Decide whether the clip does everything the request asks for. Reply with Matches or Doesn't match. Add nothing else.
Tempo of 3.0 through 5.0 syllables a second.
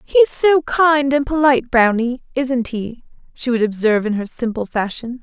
Matches